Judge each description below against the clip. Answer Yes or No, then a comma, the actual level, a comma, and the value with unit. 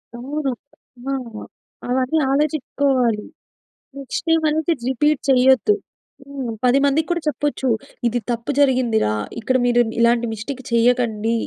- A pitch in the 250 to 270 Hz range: Yes, very high, 260 Hz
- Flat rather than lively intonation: No, average, 3.3 semitones